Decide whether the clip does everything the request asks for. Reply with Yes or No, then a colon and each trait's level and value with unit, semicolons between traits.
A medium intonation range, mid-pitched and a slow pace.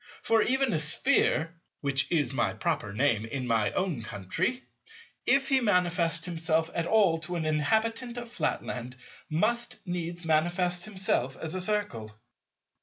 No: wide, 6.6 semitones; medium, 170 Hz; slow, 130 wpm